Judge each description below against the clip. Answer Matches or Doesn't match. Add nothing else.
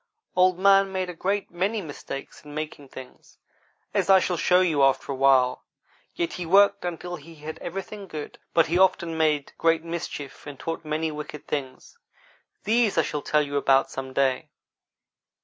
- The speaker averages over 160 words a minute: Matches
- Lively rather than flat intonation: Doesn't match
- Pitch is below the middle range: Doesn't match